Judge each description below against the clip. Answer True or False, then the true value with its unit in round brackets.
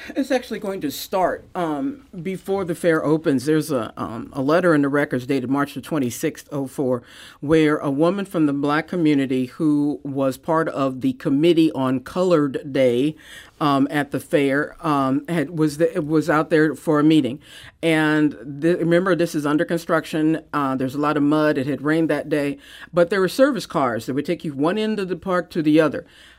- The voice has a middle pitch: True (155 Hz)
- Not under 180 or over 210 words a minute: True (200 wpm)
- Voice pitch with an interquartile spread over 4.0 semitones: False (3.1 semitones)